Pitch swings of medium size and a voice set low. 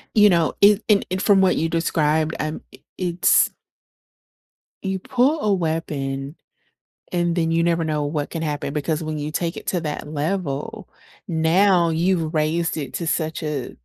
No: average, 3.1 semitones; medium, 165 Hz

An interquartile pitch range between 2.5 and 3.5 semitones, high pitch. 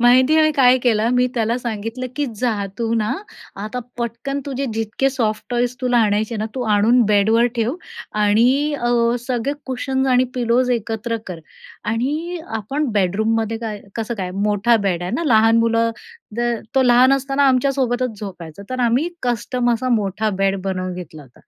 Yes: average, 3.0 semitones; high, 235 Hz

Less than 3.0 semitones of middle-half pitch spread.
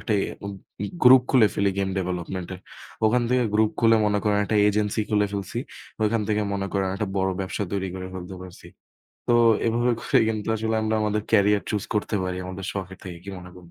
Yes: narrow, 2.5 semitones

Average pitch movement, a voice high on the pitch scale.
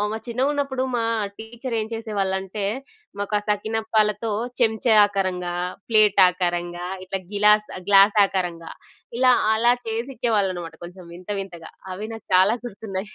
Yes: average, 3.1 semitones; high, 210 Hz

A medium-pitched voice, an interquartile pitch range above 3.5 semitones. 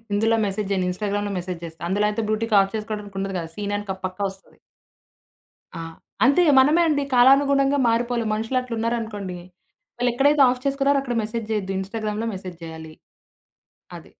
No: high, 215 Hz; average, 4.1 semitones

